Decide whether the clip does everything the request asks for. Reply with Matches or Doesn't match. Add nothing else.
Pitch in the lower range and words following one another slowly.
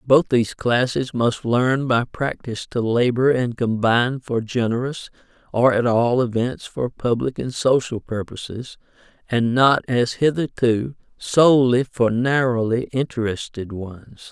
Matches